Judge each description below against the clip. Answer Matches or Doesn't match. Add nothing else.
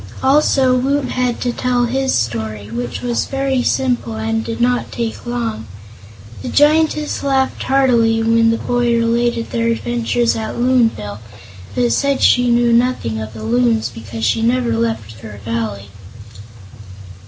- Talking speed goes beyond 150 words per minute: Doesn't match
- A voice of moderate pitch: Doesn't match